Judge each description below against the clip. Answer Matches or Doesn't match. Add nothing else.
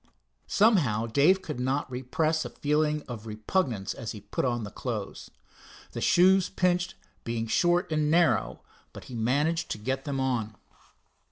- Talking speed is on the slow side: Doesn't match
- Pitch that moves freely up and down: Matches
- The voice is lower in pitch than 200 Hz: Matches